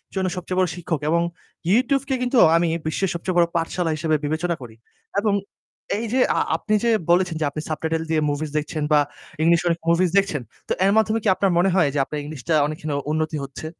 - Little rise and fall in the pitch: No, average, 3.3 semitones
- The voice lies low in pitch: No, medium, 170 Hz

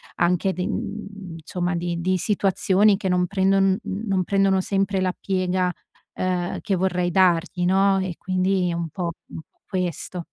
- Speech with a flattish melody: Yes, narrow, 1.5 semitones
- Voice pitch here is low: No, medium, 185 Hz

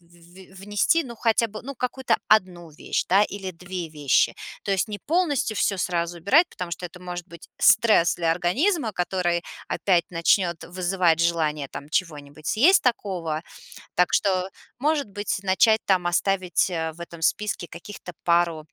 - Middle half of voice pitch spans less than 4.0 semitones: Yes, average, 3.6 semitones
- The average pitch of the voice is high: No, medium, 180 Hz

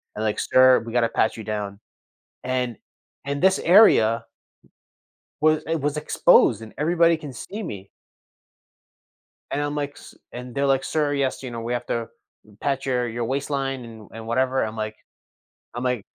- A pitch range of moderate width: Yes, average, 4.0 semitones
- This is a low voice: Yes, low, 130 Hz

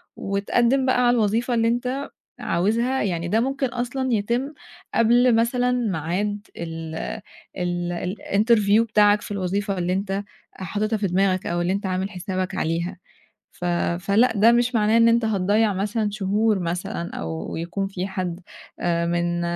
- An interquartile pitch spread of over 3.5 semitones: Yes, average, 4.2 semitones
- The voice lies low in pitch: No, high, 205 Hz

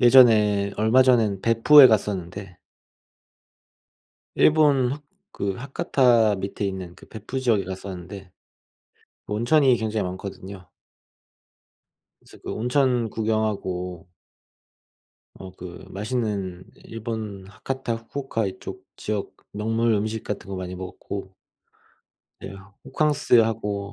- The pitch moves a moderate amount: Yes, average, 3.7 semitones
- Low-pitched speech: Yes, low, 105 Hz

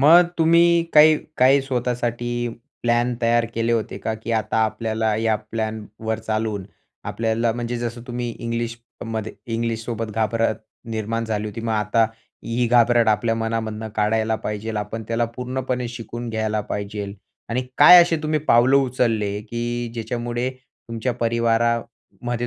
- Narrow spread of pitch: Yes, narrow, 1.5 semitones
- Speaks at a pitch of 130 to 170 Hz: No, low, 115 Hz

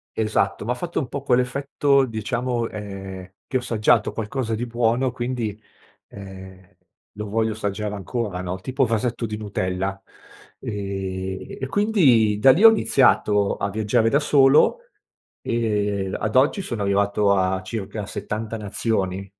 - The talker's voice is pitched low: Yes, low, 110 Hz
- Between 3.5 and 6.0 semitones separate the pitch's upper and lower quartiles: Yes, average, 3.9 semitones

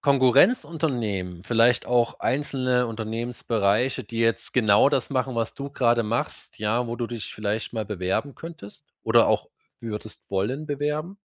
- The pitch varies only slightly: No, average, 3.7 semitones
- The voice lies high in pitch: No, low, 120 Hz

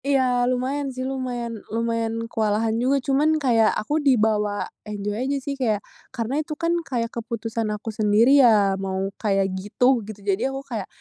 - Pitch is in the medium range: No, high, 230 Hz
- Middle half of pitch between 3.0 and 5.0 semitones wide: Yes, average, 3.3 semitones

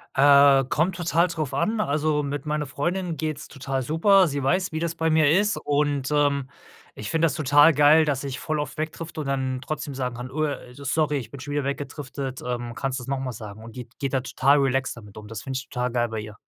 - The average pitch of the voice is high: No, medium, 140 Hz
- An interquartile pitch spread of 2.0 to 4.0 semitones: Yes, average, 3.0 semitones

